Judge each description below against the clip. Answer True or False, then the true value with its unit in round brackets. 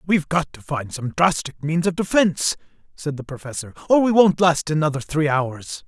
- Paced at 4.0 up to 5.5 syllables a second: True (5.3 syllables/s)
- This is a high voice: False (160 Hz)